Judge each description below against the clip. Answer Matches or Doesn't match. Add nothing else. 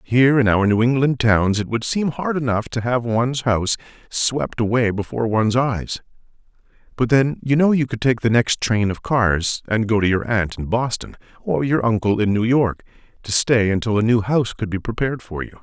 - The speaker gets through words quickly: Matches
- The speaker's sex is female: Doesn't match